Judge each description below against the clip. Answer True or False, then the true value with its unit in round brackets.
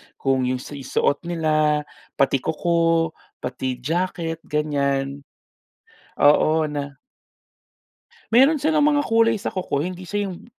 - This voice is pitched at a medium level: True (155 Hz)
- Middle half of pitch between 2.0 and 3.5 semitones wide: False (4.6 semitones)